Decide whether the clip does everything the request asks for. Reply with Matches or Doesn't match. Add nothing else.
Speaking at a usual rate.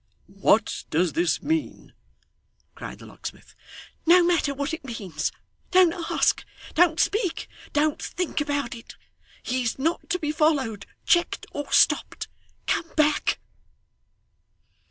Doesn't match